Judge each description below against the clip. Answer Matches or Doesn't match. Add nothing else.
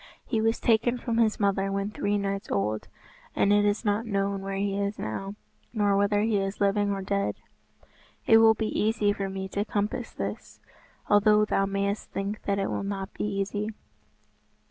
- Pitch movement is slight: Matches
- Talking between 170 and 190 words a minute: Matches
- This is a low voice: Doesn't match